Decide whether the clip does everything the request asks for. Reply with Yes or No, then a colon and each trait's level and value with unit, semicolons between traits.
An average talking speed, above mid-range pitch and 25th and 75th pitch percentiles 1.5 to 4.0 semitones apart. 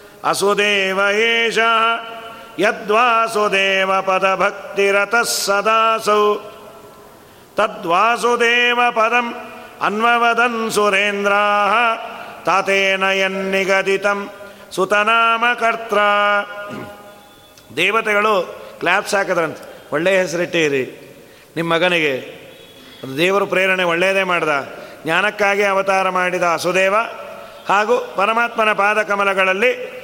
No: slow, 60 wpm; high, 205 Hz; average, 2.9 semitones